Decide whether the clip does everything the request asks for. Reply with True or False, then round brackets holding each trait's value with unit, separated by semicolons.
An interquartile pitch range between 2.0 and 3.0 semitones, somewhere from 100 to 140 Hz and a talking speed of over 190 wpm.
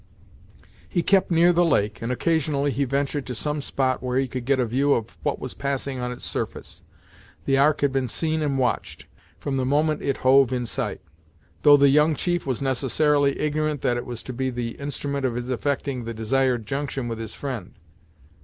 True (2.7 semitones; 135 Hz; 200 wpm)